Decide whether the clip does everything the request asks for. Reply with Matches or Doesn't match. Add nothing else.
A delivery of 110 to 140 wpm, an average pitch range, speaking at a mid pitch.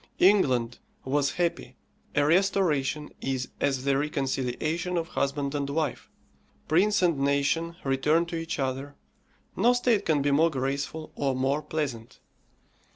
Matches